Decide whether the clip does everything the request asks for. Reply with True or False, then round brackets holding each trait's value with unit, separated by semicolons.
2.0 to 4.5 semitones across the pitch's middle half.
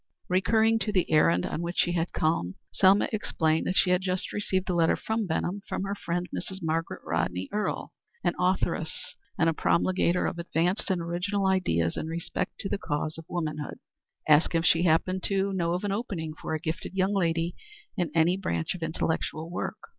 True (2.8 semitones)